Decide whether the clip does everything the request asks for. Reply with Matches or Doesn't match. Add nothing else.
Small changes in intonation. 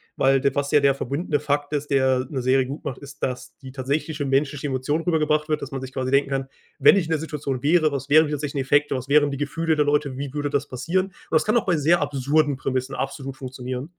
Matches